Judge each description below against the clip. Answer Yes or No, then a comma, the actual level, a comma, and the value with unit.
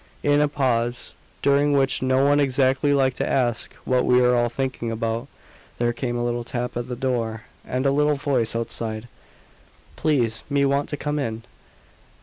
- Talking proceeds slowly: No, average, 175 wpm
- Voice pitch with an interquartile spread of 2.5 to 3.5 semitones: Yes, average, 2.8 semitones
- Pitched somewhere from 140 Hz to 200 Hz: No, low, 130 Hz